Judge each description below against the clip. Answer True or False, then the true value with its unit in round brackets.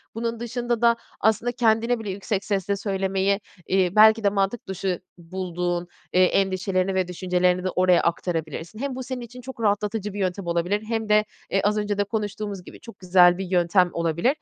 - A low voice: False (195 Hz)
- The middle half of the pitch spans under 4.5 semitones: True (3.2 semitones)